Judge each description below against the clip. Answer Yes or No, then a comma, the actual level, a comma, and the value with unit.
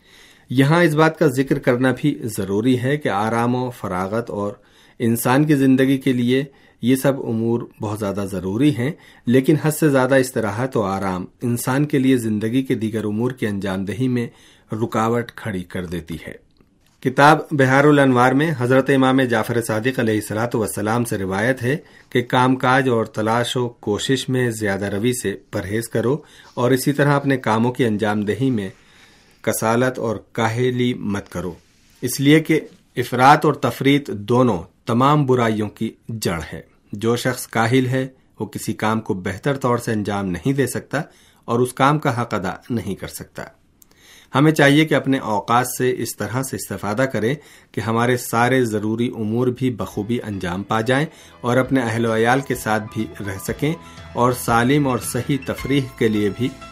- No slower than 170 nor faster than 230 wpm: Yes, average, 175 wpm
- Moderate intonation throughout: Yes, average, 3.7 semitones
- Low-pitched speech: Yes, low, 120 Hz